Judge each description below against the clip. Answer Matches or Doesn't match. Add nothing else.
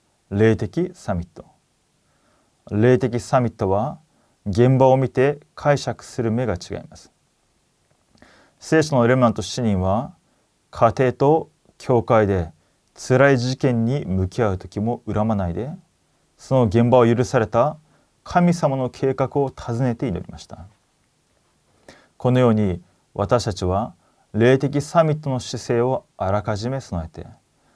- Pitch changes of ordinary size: Matches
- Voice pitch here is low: Matches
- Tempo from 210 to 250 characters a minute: Matches